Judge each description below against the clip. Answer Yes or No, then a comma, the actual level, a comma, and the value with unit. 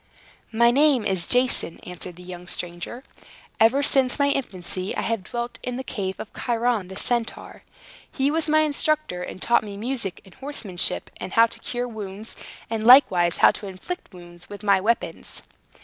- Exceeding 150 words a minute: Yes, average, 175 wpm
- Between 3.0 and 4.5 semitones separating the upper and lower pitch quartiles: No, average, 5.3 semitones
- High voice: Yes, high, 225 Hz